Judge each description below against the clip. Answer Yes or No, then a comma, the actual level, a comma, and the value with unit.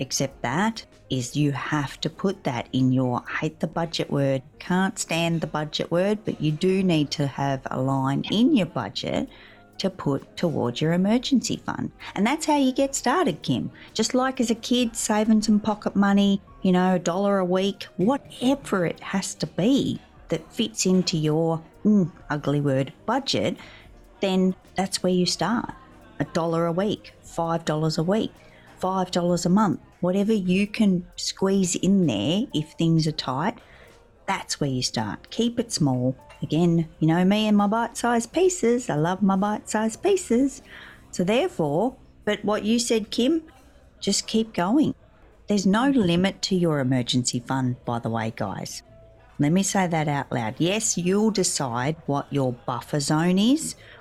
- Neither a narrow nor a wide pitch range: No, wide, 6.1 semitones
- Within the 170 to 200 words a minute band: Yes, average, 175 wpm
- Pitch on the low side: No, medium, 180 Hz